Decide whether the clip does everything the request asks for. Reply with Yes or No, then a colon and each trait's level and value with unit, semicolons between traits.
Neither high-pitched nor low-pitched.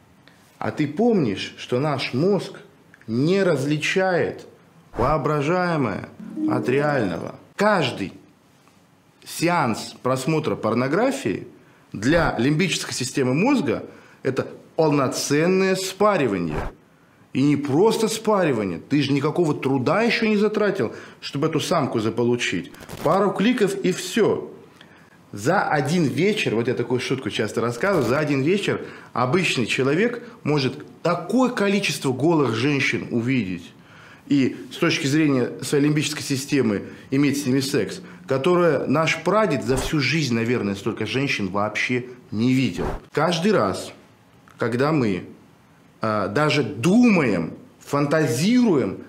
Yes: medium, 145 Hz